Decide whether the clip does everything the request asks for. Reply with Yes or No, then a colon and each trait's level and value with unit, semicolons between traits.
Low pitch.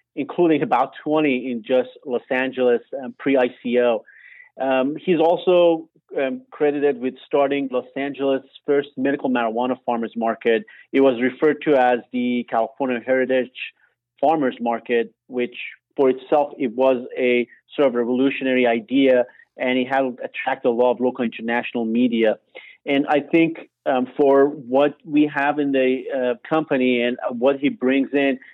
Yes: low, 130 Hz